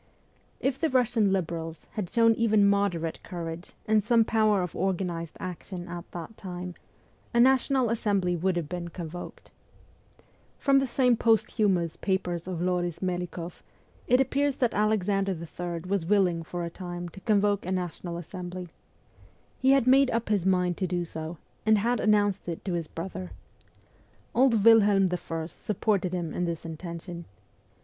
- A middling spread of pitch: Yes, average, 3.8 semitones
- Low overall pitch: No, medium, 185 Hz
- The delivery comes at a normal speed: Yes, average, 155 wpm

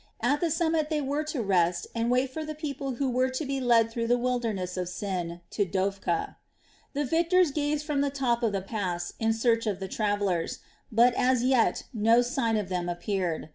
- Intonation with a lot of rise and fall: Yes, wide, 5.9 semitones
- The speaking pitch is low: No, high, 235 Hz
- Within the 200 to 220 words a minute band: Yes, fast, 205 wpm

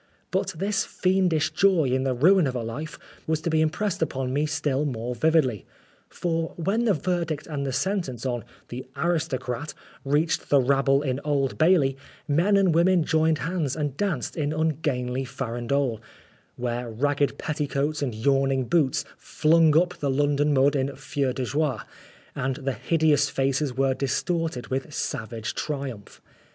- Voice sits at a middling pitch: Yes, medium, 145 Hz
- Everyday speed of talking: Yes, average, 160 wpm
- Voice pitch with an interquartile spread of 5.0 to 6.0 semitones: No, average, 3.4 semitones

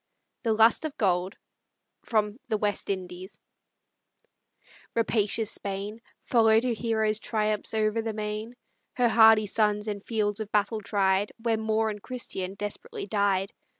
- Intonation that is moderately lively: No, narrow, 1.7 semitones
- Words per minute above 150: No, slow, 135 wpm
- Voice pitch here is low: No, high, 215 Hz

